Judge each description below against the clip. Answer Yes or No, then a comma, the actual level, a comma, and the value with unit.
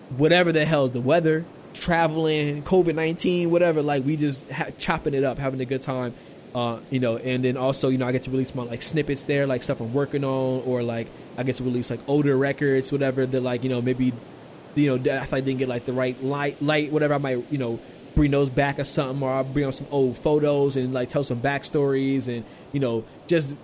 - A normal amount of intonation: No, narrow, 2.3 semitones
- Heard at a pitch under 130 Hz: No, low, 135 Hz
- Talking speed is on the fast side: Yes, fast, 240 wpm